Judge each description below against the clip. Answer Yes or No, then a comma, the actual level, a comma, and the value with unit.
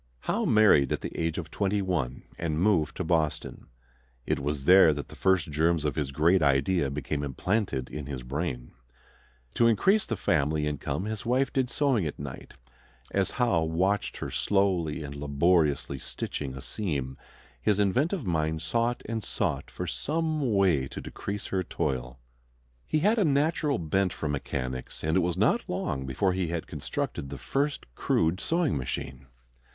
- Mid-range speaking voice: No, very low, 85 Hz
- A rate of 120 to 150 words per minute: No, average, 165 wpm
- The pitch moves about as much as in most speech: No, wide, 6.6 semitones